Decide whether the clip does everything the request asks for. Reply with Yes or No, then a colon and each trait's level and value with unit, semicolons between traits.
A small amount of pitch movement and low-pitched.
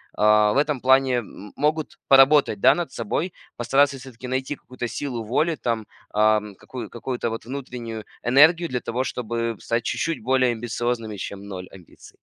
No: average, 3.3 semitones; low, 120 Hz